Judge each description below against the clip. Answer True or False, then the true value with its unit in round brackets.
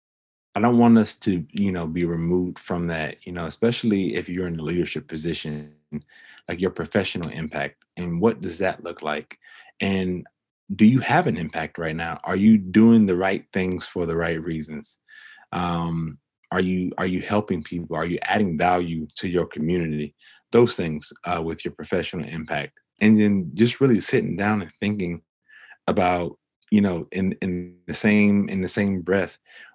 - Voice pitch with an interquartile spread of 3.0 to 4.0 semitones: True (3.6 semitones)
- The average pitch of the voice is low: True (90 Hz)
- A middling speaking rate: True (175 wpm)